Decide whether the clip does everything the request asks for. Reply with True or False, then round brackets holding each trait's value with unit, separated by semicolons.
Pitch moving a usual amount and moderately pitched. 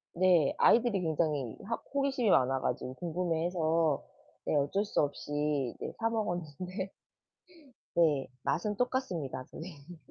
True (4.7 semitones; 165 Hz)